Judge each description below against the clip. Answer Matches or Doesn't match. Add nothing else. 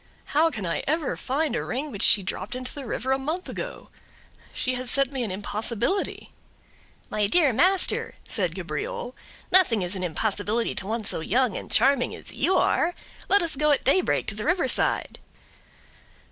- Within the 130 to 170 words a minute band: Doesn't match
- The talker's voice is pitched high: Matches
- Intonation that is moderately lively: Doesn't match